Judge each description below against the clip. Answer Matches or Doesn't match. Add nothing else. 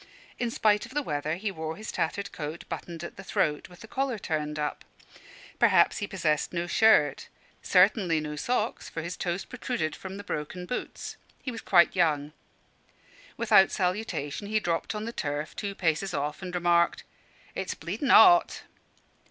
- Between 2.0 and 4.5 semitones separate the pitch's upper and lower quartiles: Doesn't match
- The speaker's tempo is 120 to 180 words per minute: Matches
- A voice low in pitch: Doesn't match